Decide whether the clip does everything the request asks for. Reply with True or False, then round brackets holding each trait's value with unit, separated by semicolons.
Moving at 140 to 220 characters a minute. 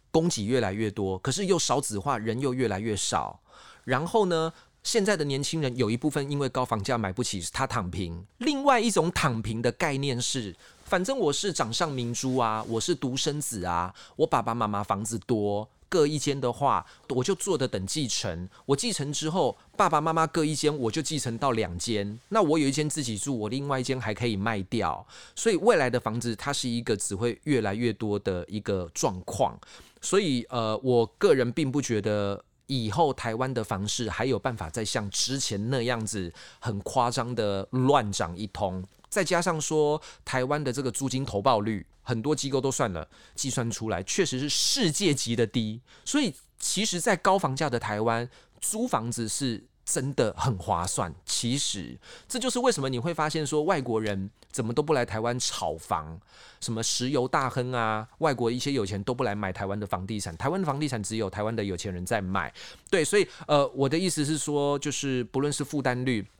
False (285 characters per minute)